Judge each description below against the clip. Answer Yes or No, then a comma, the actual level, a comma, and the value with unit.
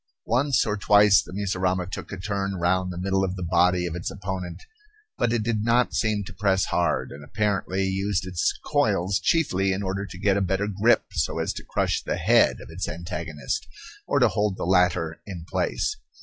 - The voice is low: Yes, very low, 95 Hz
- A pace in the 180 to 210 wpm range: Yes, average, 200 wpm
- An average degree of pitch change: No, narrow, 2.2 semitones